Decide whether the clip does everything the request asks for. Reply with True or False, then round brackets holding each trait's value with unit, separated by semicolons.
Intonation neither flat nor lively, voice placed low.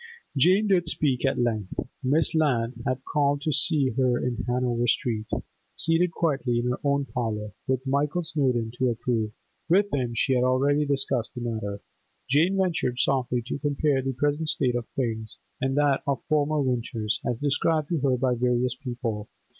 True (3.4 semitones; 130 Hz)